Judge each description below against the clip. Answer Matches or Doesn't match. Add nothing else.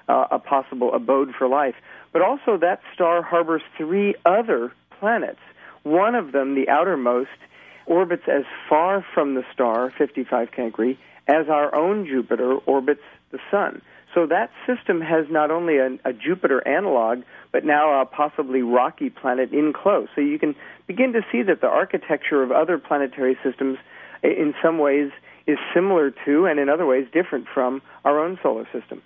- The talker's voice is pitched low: Doesn't match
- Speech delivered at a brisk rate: Doesn't match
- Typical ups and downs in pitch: Matches